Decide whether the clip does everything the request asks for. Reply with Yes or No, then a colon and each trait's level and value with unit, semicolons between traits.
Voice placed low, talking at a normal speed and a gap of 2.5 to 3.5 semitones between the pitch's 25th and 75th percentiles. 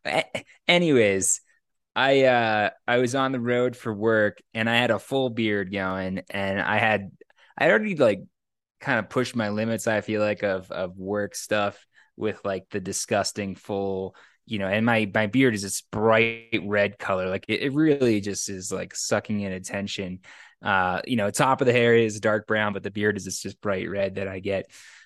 Yes: low, 105 Hz; average, 195 wpm; average, 2.8 semitones